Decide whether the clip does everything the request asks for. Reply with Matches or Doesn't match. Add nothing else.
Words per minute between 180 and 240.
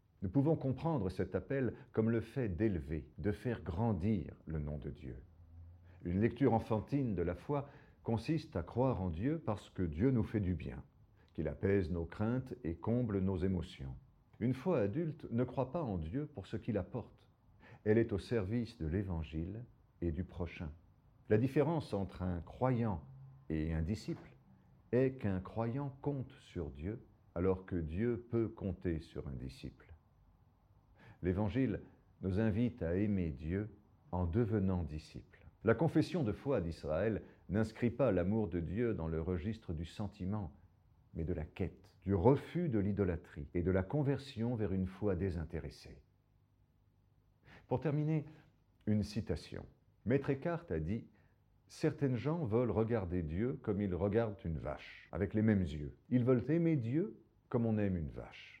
Doesn't match